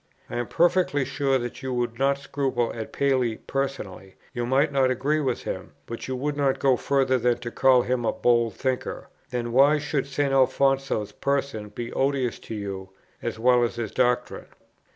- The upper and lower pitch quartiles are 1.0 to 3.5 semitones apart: Yes, narrow, 2.5 semitones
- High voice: No, low, 130 Hz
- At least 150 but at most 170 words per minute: No, average, 185 wpm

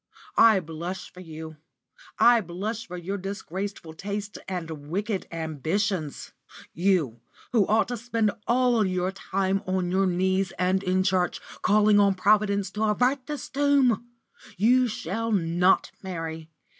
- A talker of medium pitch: No, high, 195 Hz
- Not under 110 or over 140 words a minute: Yes, slow, 135 wpm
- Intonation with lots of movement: No, average, 3.3 semitones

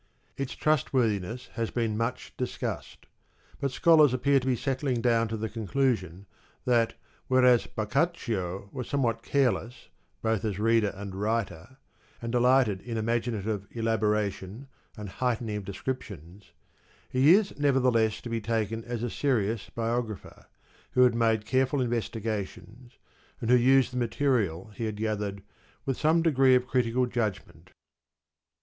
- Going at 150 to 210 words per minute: No, slow, 135 wpm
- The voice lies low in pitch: Yes, low, 115 Hz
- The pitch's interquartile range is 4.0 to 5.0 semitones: No, average, 3.1 semitones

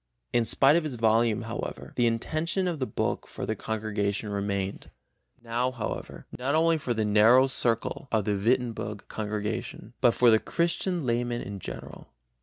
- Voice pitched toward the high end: No, low, 115 Hz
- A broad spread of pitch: No, average, 3.3 semitones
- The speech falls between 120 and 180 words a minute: Yes, average, 165 wpm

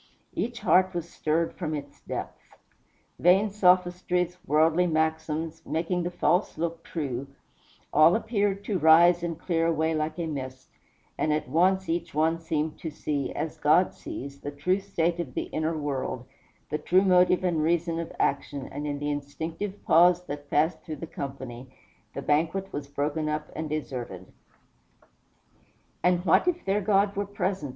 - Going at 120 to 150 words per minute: No, average, 160 wpm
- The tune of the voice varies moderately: Yes, average, 3.2 semitones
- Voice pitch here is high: No, medium, 165 Hz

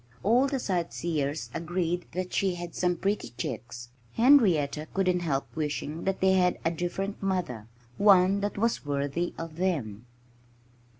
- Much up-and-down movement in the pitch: No, average, 4.2 semitones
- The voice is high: No, medium, 175 Hz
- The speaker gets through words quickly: No, average, 140 wpm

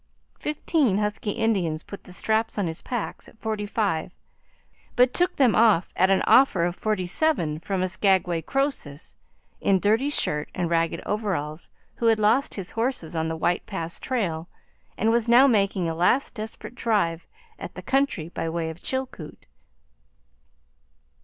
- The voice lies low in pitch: No, high, 200 Hz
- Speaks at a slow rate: No, average, 160 wpm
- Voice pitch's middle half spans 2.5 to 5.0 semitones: No, wide, 5.5 semitones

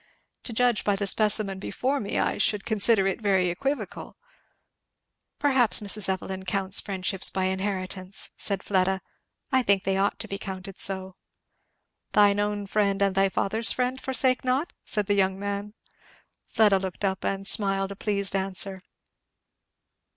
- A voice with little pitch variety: Yes, narrow, 1.7 semitones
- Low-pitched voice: No, high, 200 Hz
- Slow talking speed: No, average, 150 wpm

